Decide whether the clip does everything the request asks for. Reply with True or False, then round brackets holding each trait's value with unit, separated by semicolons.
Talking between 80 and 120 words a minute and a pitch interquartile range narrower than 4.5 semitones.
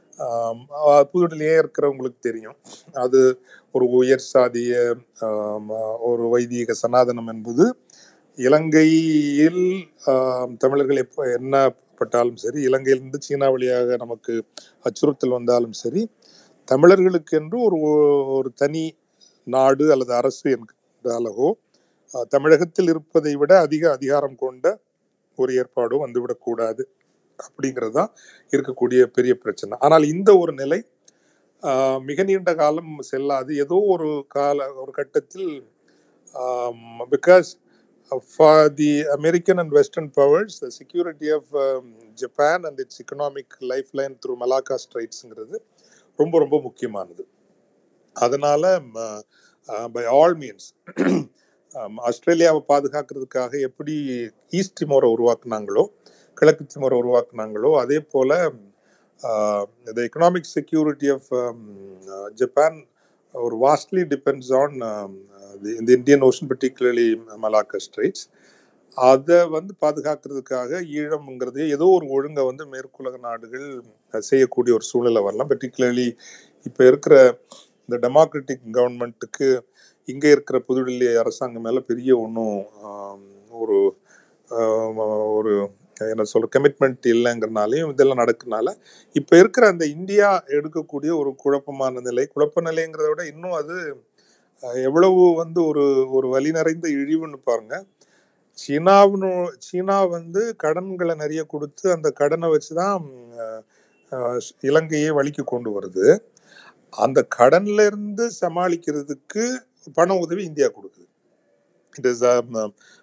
False (95 wpm; 5.5 semitones)